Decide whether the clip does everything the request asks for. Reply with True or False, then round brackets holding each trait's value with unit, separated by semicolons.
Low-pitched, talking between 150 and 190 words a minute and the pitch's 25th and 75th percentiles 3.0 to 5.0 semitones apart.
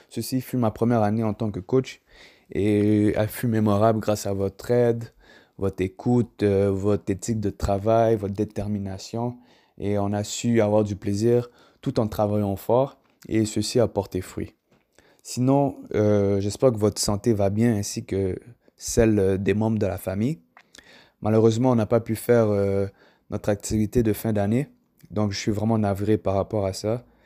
False (105 Hz; 170 wpm; 2.4 semitones)